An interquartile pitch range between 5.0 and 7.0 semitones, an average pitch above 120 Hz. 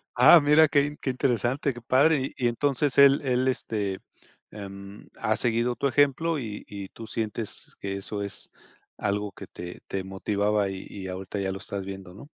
No: average, 5.3 semitones; low, 110 Hz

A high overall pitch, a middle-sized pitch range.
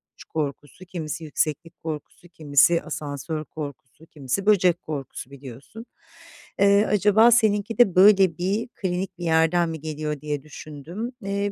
No: medium, 165 Hz; average, 4.7 semitones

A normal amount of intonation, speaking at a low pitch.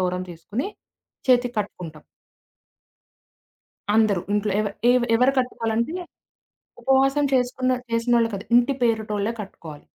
No: average, 3.7 semitones; high, 230 Hz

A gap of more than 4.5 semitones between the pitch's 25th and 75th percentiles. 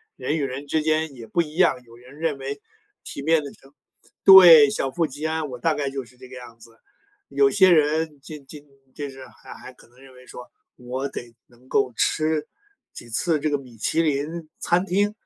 No: average, 3.7 semitones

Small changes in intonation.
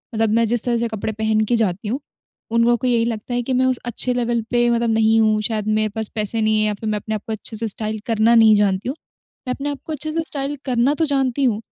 Yes: narrow, 2.3 semitones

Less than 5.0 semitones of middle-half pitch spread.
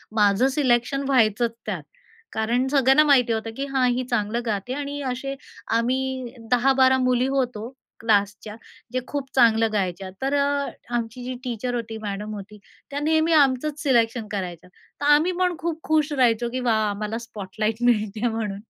Yes: average, 3.7 semitones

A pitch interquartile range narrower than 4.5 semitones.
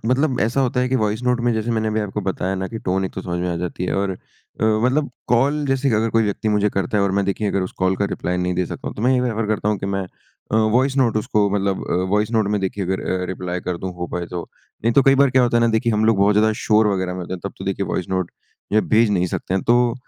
Yes: average, 3.8 semitones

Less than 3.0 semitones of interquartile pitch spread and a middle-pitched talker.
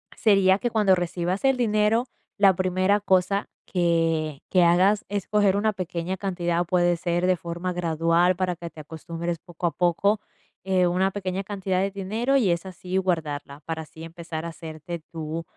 Yes: narrow, 2.6 semitones; medium, 180 Hz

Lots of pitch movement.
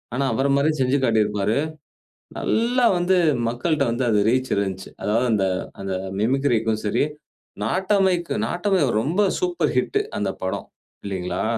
Yes: wide, 8.7 semitones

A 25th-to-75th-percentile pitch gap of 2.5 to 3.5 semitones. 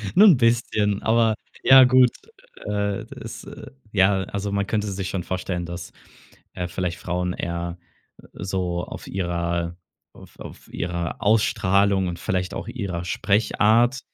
Yes: average, 3.2 semitones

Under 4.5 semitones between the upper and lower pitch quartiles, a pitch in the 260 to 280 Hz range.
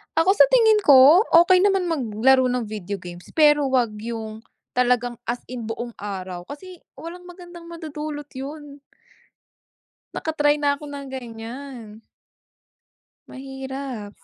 No: average, 5.0 semitones; very high, 265 Hz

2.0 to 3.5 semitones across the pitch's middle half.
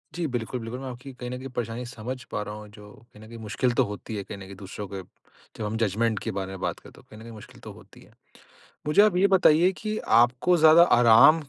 No: average, 4.0 semitones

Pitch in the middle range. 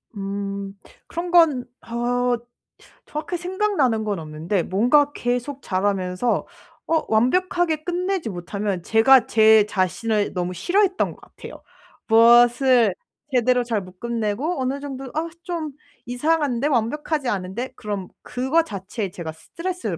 No: high, 240 Hz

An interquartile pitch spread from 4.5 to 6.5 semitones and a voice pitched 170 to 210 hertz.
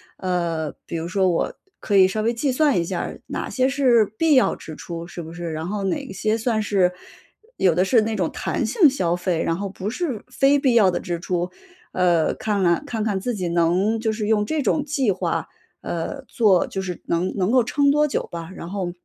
Yes: average, 5.3 semitones; high, 195 Hz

